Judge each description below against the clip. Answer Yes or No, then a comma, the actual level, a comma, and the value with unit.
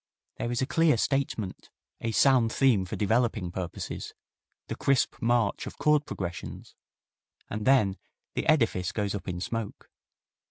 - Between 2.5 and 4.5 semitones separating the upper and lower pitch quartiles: No, average, 5.1 semitones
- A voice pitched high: No, low, 115 Hz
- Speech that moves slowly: No, average, 145 wpm